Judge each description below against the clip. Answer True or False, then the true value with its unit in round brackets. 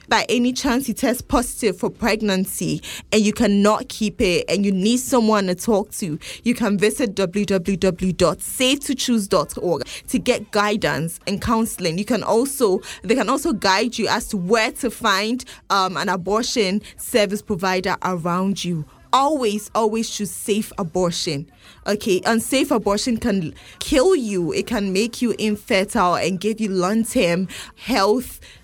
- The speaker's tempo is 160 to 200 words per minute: False (145 wpm)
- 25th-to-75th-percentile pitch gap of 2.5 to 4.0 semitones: True (3.4 semitones)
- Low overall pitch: False (210 Hz)